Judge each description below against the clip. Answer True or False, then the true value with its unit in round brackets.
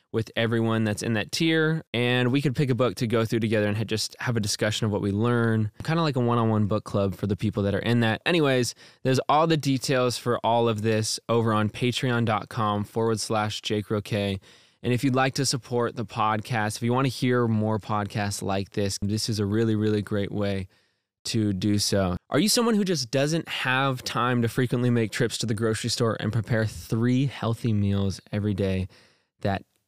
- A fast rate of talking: True (215 wpm)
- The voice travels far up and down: False (2.8 semitones)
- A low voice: True (115 Hz)